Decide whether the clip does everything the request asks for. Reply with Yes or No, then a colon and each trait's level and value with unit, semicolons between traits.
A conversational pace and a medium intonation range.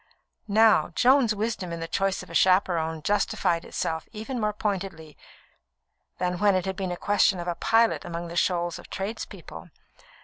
Yes: average, 165 wpm; average, 3.5 semitones